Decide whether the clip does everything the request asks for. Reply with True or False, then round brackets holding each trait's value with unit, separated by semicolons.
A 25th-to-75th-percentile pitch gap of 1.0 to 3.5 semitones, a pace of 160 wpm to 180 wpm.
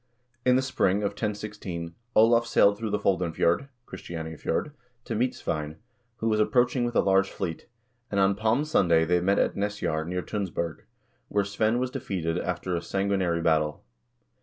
False (4.5 semitones; 165 wpm)